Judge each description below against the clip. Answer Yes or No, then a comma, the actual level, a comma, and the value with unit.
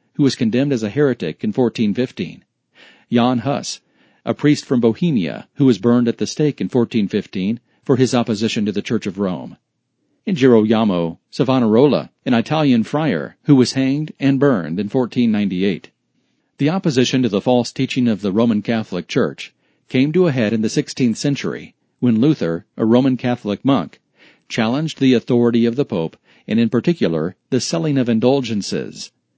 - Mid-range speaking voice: No, low, 125 Hz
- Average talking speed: Yes, average, 165 wpm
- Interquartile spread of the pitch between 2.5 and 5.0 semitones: Yes, average, 3.7 semitones